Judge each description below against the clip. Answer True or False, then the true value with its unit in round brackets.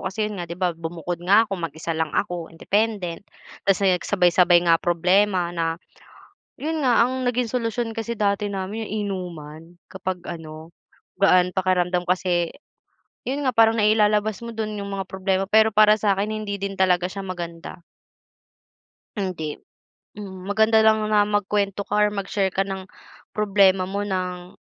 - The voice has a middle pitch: False (195 Hz)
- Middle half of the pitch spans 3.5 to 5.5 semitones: False (3.1 semitones)